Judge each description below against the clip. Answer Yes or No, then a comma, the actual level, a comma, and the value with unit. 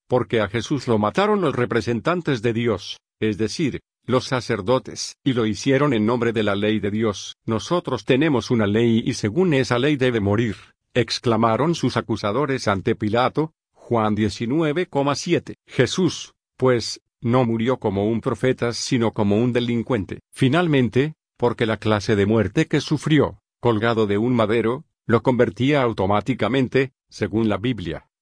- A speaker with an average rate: Yes, average, 145 wpm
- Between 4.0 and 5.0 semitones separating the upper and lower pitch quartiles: No, average, 3.2 semitones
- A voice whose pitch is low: Yes, low, 120 Hz